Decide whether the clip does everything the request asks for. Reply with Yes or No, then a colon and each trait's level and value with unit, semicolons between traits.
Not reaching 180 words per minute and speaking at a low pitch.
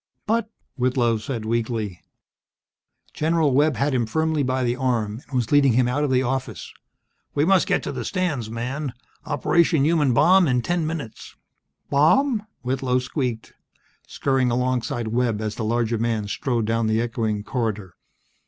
Yes: average, 160 wpm; low, 125 Hz